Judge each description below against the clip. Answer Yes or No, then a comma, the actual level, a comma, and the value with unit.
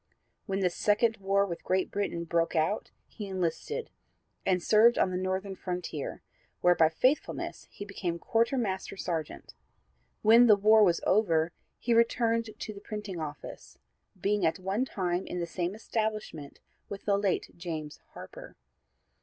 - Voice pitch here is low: No, high, 195 Hz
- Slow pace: No, average, 150 wpm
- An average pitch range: Yes, average, 3.6 semitones